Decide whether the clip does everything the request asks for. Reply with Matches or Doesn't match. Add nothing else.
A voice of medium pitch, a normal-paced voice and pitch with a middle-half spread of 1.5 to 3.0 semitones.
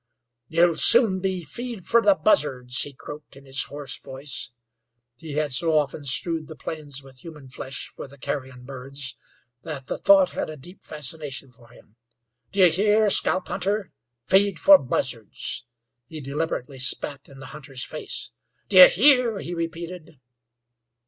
Doesn't match